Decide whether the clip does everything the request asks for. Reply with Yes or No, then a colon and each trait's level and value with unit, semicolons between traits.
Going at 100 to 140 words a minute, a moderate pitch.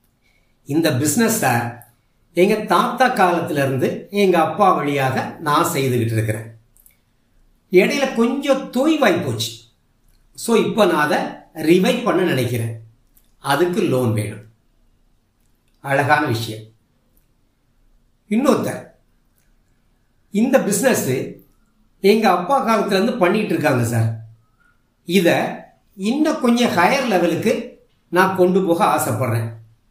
No: average, 85 wpm; medium, 155 Hz